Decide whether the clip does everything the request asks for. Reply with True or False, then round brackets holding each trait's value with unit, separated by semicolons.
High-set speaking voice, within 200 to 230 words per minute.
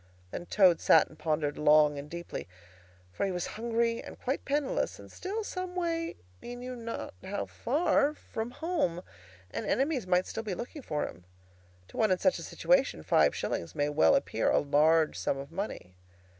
False (200 Hz; 180 wpm)